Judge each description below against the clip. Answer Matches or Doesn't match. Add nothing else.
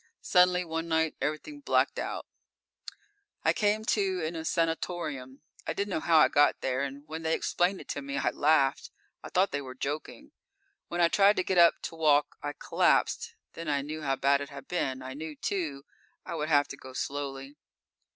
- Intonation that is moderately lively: Matches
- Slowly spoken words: Doesn't match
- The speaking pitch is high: Doesn't match